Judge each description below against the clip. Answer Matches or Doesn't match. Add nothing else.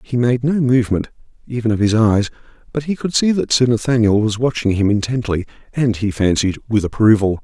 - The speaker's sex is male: Matches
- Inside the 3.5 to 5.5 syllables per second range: Doesn't match